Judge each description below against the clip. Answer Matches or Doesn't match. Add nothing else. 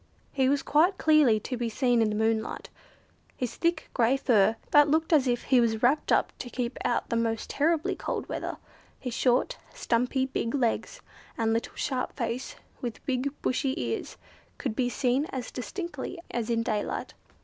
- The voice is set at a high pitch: Matches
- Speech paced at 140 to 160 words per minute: Doesn't match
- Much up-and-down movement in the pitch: Doesn't match